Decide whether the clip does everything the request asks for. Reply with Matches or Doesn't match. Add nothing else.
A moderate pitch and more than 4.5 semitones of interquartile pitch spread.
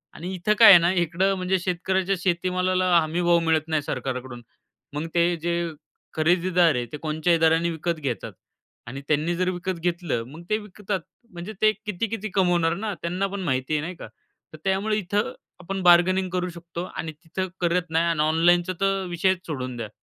Doesn't match